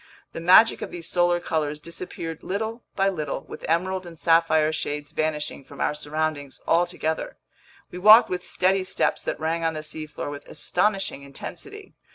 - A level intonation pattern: No, average, 3.2 semitones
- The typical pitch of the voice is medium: Yes, medium, 165 Hz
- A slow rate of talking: No, average, 165 wpm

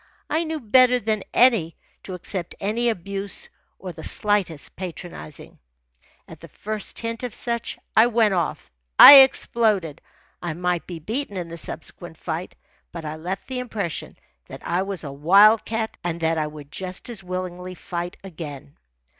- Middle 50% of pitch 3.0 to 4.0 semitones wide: No, average, 4.8 semitones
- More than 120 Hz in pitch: Yes, medium, 185 Hz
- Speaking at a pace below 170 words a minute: Yes, average, 160 wpm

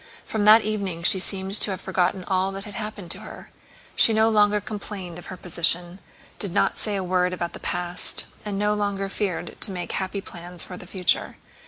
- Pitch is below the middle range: No, high, 195 Hz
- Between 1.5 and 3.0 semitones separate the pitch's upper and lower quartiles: Yes, narrow, 2.5 semitones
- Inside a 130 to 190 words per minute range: No, fast, 205 wpm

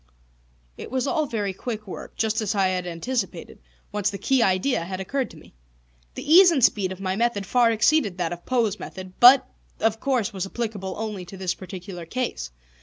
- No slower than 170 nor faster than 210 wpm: Yes, average, 195 wpm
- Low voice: No, high, 210 Hz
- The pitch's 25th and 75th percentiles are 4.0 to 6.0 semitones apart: Yes, average, 4.7 semitones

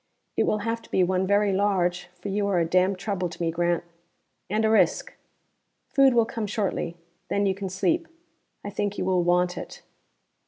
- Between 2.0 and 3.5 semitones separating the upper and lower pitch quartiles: Yes, narrow, 2.6 semitones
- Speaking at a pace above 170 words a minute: Yes, average, 195 wpm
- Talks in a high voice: Yes, high, 195 Hz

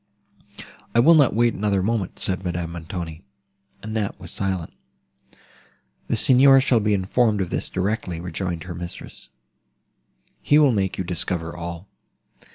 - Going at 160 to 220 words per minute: No, average, 140 wpm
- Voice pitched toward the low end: Yes, very low, 95 Hz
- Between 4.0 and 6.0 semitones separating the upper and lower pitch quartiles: Yes, average, 4.3 semitones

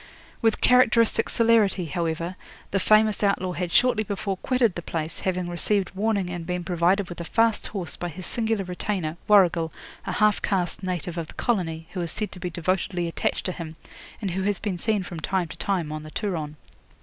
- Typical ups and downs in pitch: Yes, average, 3.5 semitones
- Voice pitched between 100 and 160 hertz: No, medium, 185 Hz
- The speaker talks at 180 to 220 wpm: Yes, average, 195 wpm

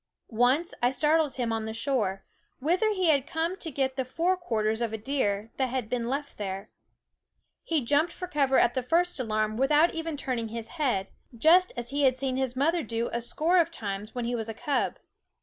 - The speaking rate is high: Yes, fast, 210 wpm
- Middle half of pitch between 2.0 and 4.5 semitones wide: No, wide, 5.5 semitones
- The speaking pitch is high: Yes, very high, 260 Hz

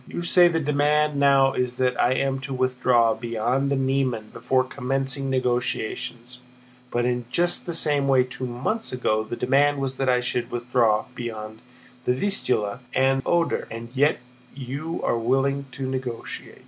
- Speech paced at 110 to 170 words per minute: Yes, average, 165 wpm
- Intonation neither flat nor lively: No, narrow, 2.1 semitones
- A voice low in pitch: Yes, low, 130 Hz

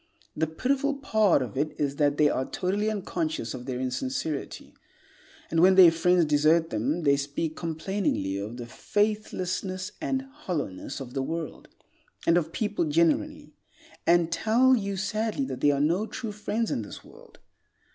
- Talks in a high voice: No, medium, 165 Hz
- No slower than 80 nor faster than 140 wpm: No, average, 160 wpm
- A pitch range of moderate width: No, wide, 6.3 semitones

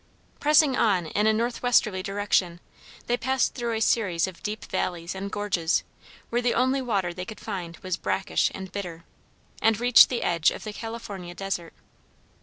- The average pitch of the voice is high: Yes, high, 205 Hz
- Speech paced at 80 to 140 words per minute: No, average, 170 wpm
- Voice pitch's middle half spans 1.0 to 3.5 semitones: No, average, 4.5 semitones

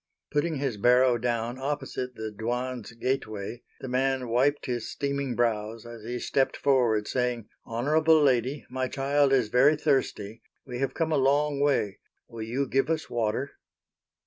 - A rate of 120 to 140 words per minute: No, average, 155 wpm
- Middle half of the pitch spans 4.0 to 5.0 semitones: No, average, 3.0 semitones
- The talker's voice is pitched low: Yes, low, 125 Hz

